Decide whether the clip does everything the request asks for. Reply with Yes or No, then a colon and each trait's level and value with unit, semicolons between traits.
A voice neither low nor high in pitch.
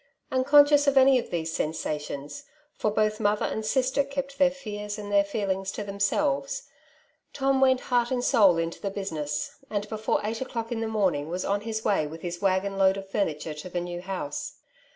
No: high, 205 Hz